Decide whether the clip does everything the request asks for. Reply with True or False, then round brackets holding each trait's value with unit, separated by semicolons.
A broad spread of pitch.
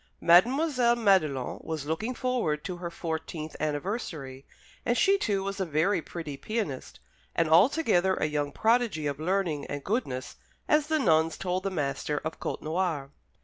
True (6.3 semitones)